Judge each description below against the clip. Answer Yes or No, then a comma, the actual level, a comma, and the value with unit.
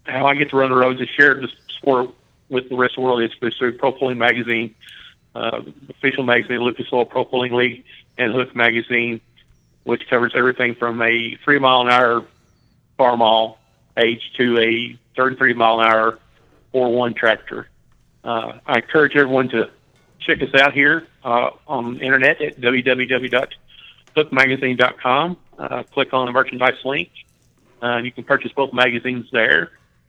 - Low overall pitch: Yes, low, 125 Hz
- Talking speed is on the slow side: No, average, 165 wpm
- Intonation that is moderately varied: No, narrow, 2.0 semitones